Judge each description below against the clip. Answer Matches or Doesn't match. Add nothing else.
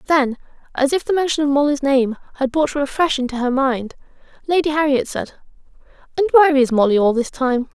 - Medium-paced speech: Matches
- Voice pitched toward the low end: Doesn't match